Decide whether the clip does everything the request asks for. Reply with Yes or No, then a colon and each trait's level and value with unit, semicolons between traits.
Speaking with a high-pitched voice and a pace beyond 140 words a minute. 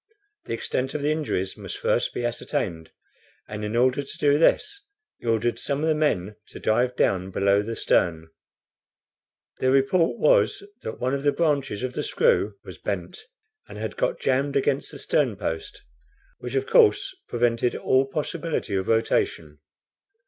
No: low, 130 Hz; average, 165 wpm